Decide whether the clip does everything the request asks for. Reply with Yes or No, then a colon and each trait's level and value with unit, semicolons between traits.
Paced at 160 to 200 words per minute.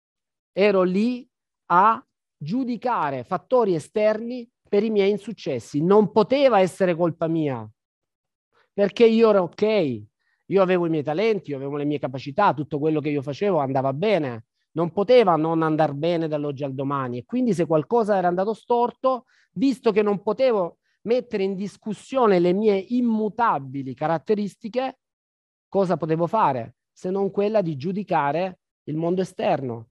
No: average, 145 wpm